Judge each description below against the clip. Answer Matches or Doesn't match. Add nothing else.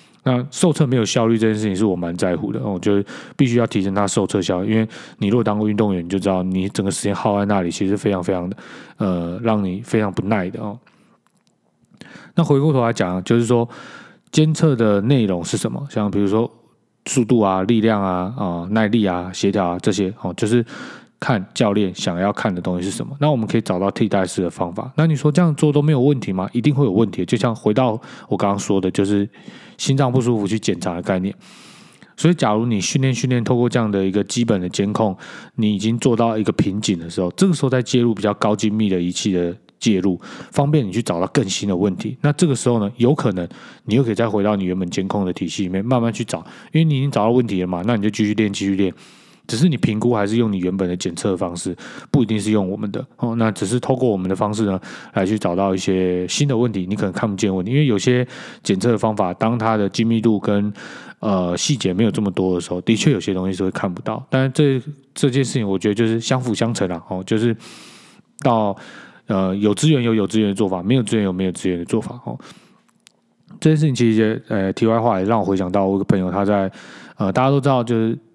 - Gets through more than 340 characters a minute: Matches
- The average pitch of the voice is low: Matches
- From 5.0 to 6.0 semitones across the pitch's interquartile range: Doesn't match